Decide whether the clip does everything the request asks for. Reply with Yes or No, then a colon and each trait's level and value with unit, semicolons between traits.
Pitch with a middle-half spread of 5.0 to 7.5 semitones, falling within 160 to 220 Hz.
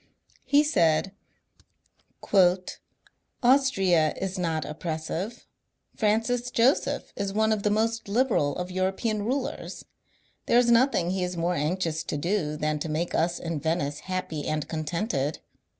Yes: wide, 5.4 semitones; medium, 185 Hz